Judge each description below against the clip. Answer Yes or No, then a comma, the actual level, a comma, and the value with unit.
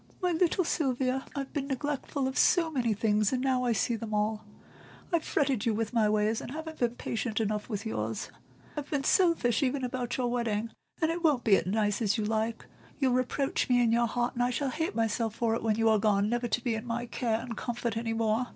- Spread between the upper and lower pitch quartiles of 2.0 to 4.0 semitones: Yes, average, 3.3 semitones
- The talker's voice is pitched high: Yes, high, 240 Hz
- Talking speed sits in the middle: No, fast, 225 wpm